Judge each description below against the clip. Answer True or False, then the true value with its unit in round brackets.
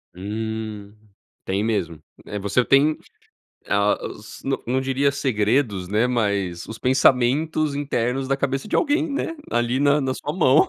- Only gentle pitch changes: False (5.1 semitones)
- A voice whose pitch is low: True (125 Hz)